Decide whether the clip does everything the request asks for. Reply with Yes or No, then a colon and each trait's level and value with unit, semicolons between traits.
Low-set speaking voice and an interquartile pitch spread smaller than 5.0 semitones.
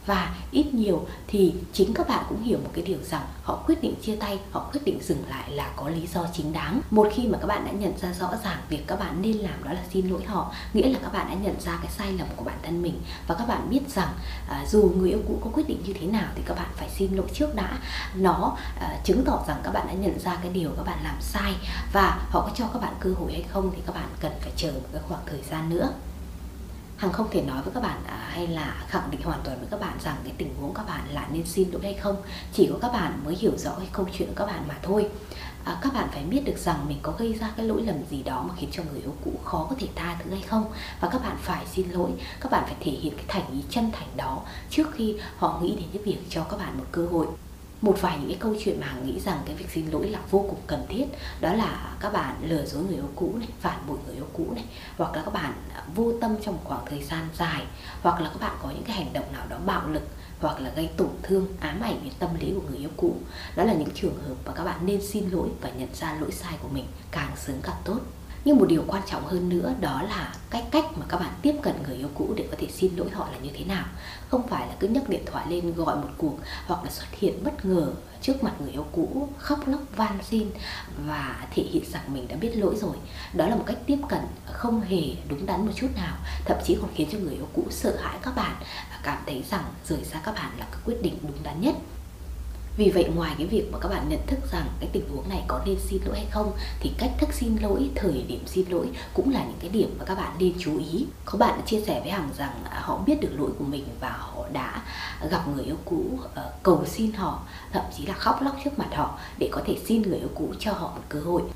No: high, 190 Hz; average, 4.6 semitones